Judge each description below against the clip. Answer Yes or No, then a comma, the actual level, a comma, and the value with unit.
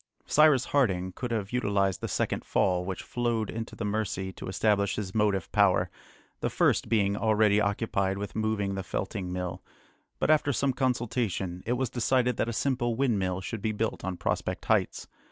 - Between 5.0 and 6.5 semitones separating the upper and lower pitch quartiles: No, average, 3.8 semitones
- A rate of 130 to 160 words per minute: No, average, 175 wpm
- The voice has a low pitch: Yes, low, 105 Hz